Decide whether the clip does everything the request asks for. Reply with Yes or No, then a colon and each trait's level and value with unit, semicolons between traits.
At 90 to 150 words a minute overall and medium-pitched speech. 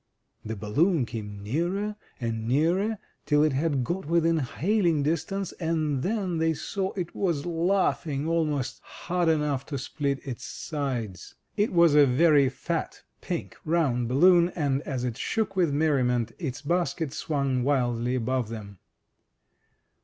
Yes: average, 140 wpm; medium, 150 Hz